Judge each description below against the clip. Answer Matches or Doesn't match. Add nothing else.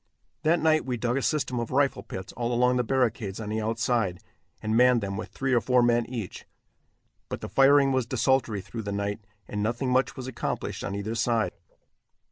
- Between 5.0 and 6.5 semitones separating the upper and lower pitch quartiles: Doesn't match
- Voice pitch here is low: Matches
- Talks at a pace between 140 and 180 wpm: Doesn't match